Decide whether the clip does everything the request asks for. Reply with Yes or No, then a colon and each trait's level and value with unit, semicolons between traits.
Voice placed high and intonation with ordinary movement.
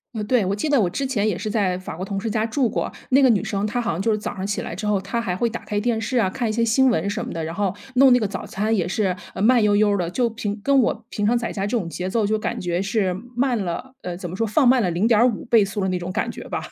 Yes: high, 210 Hz; average, 3.5 semitones